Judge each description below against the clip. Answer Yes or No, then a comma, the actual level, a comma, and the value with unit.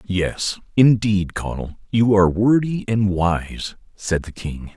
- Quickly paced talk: No, average, 140 wpm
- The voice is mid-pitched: No, low, 100 Hz